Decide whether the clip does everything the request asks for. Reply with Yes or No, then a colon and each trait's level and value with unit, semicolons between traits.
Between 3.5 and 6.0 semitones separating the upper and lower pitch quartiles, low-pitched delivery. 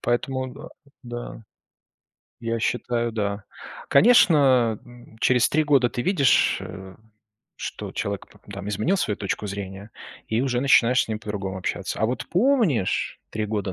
Yes: average, 4.3 semitones; low, 120 Hz